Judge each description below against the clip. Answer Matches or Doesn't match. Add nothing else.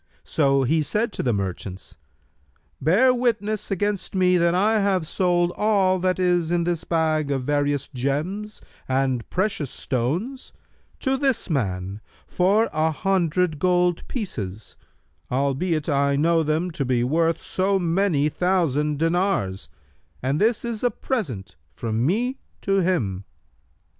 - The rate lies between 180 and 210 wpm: Doesn't match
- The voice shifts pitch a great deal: Matches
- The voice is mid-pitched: Matches